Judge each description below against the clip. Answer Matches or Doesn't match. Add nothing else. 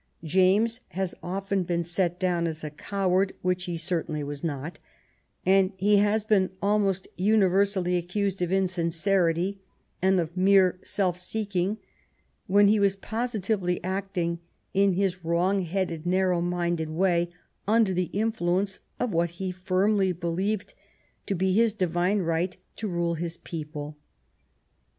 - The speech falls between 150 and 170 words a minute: Doesn't match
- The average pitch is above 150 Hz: Matches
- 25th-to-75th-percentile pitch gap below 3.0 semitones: Matches